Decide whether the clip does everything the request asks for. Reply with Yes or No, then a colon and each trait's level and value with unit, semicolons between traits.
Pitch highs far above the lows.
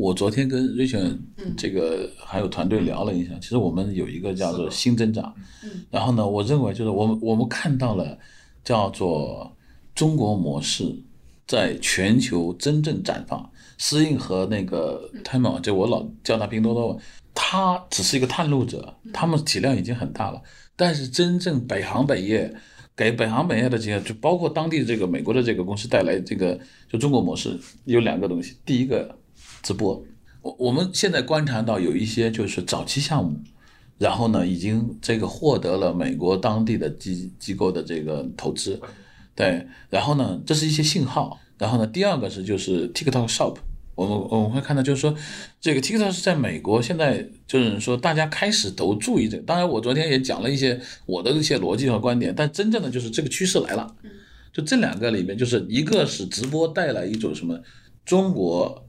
Yes: wide, 6.4 semitones